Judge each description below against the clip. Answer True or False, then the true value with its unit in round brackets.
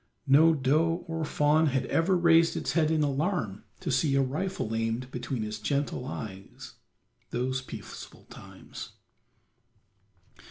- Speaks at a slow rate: True (130 wpm)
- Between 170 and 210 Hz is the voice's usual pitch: False (140 Hz)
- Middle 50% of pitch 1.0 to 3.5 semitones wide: False (4.3 semitones)